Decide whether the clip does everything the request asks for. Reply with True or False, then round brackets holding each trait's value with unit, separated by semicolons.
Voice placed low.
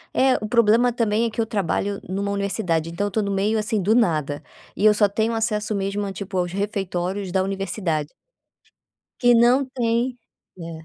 False (205 Hz)